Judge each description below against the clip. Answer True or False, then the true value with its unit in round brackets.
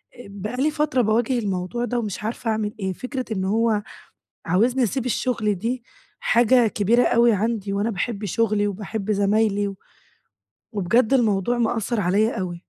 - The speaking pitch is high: True (220 Hz)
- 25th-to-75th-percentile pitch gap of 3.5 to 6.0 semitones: False (3.1 semitones)